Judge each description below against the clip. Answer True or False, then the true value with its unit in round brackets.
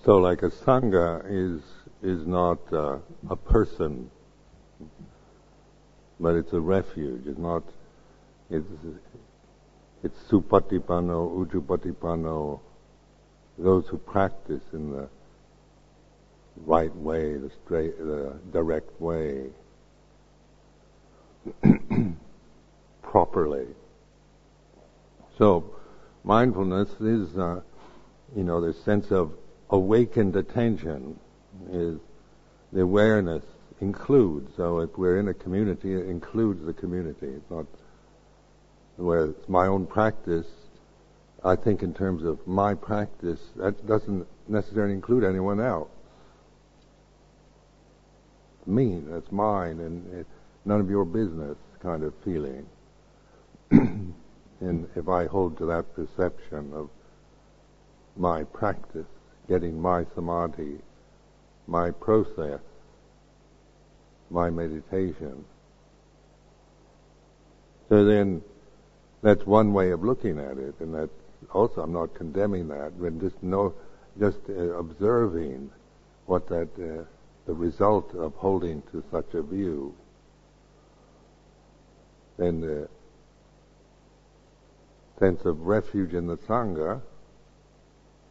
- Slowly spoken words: True (100 wpm)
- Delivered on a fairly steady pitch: False (3.4 semitones)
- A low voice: True (90 Hz)